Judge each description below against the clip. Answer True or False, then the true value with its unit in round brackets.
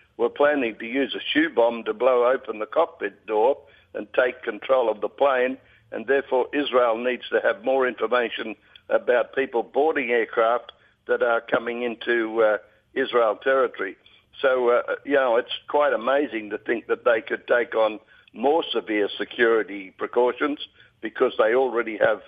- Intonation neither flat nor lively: True (3.6 semitones)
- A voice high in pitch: False (125 Hz)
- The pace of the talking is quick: False (160 wpm)